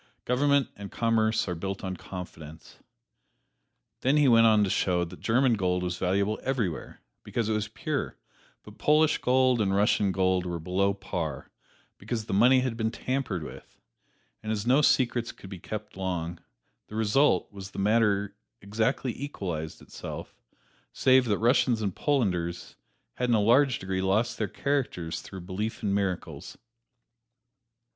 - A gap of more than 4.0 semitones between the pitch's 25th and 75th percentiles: Yes, average, 4.5 semitones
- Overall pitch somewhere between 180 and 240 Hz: No, low, 105 Hz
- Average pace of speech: Yes, average, 155 wpm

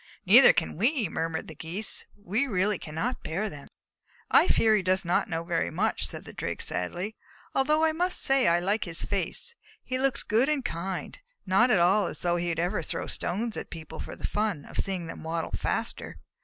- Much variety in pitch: Yes, wide, 5.7 semitones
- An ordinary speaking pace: No, fast, 210 wpm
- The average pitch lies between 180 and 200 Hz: Yes, high, 190 Hz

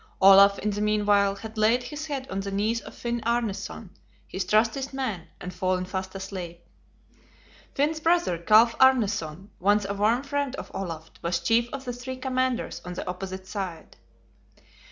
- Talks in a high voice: Yes, high, 210 Hz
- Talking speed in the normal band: Yes, average, 170 wpm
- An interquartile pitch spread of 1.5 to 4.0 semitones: No, average, 4.7 semitones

